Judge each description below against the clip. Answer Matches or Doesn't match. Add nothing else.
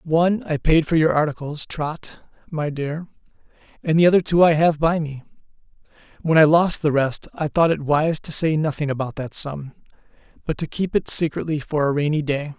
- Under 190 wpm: Doesn't match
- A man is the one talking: Matches